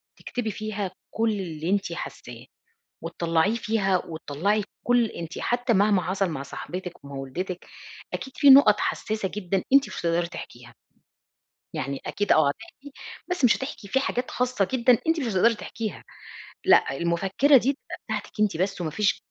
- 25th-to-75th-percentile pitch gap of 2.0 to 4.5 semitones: No, average, 5.3 semitones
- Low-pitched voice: No, high, 200 Hz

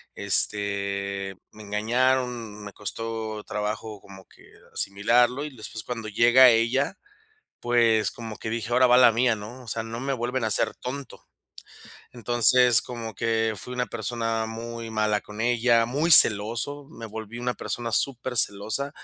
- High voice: No, low, 115 Hz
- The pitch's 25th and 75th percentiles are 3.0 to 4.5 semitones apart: No, narrow, 2.5 semitones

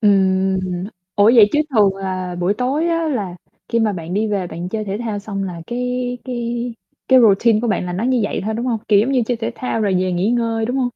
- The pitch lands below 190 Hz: No, high, 220 Hz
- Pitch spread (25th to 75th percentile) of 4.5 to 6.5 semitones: No, average, 4.0 semitones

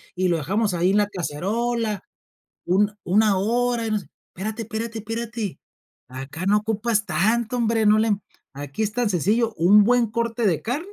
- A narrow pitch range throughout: No, average, 3.4 semitones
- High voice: Yes, high, 215 Hz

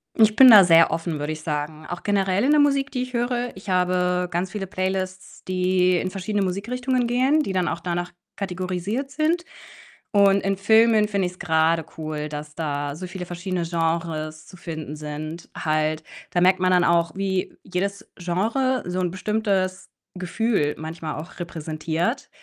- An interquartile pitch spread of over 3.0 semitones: Yes, average, 3.7 semitones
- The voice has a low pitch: No, medium, 185 Hz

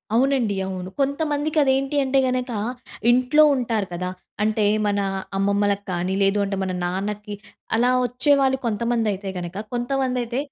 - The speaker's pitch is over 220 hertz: Yes, high, 235 Hz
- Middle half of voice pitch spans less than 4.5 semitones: No, average, 4.8 semitones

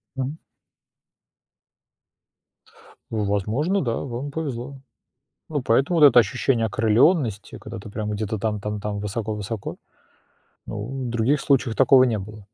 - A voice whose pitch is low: Yes, low, 115 Hz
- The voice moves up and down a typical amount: Yes, average, 4.2 semitones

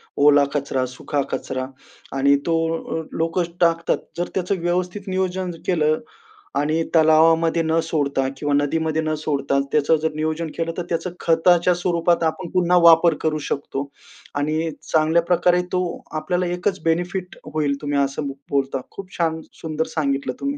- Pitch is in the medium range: Yes, medium, 160 Hz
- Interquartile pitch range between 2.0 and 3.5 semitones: Yes, average, 2.9 semitones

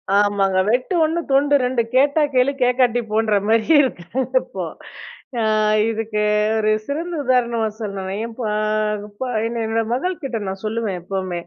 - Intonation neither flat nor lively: Yes, average, 3.6 semitones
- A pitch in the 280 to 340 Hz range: No, high, 230 Hz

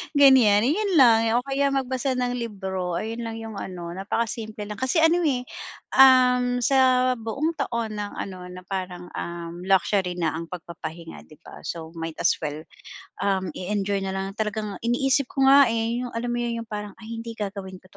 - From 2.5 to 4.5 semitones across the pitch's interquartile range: No, average, 5.0 semitones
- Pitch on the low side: No, high, 220 Hz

